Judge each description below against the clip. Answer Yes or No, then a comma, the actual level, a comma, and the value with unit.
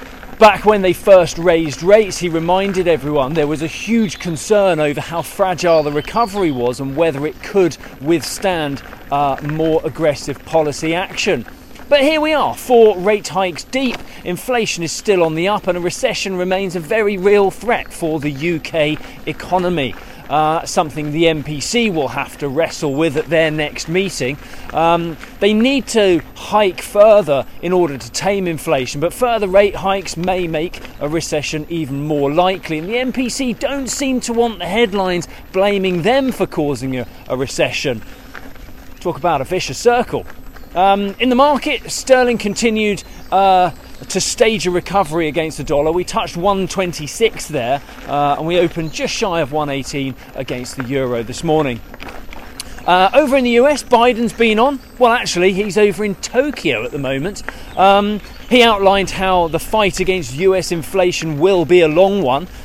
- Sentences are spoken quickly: No, average, 165 wpm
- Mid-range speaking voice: Yes, medium, 180 Hz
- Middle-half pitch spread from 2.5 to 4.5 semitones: No, average, 5.2 semitones